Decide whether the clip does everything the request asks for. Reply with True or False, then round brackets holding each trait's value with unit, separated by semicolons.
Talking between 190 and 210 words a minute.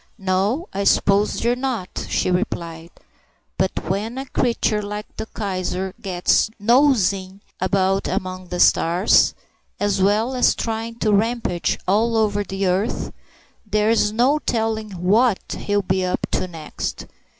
False (135 wpm)